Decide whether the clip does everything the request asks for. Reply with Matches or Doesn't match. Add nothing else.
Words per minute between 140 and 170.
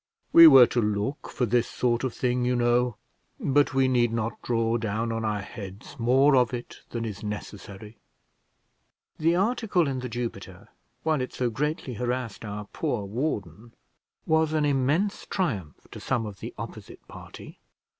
Matches